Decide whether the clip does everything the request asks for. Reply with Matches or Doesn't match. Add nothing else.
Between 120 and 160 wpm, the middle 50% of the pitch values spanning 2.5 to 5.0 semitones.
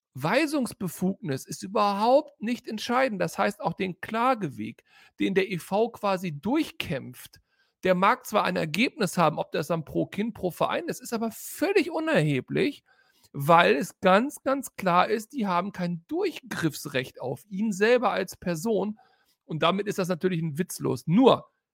Doesn't match